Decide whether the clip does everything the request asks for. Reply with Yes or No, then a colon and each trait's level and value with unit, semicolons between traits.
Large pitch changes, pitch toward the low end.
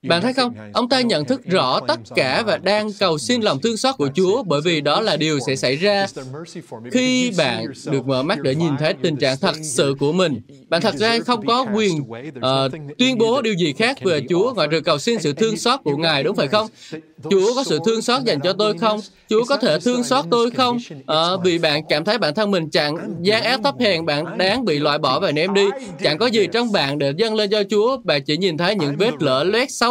No: wide, 6.9 semitones; high, 195 Hz